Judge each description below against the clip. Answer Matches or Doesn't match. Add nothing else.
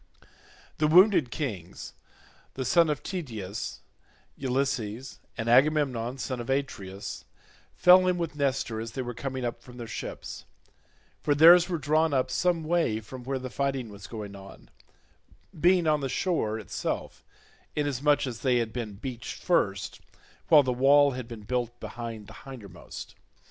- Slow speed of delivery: Doesn't match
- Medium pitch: Doesn't match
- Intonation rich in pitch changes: Doesn't match